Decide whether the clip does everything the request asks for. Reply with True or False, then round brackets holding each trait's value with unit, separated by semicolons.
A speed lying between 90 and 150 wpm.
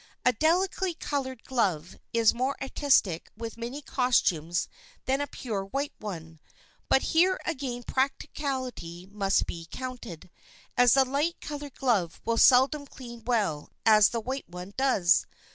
True (140 wpm)